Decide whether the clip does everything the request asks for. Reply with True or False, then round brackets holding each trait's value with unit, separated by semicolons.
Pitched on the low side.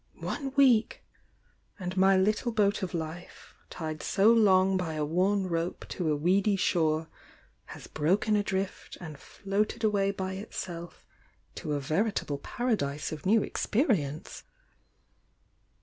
False (190 Hz)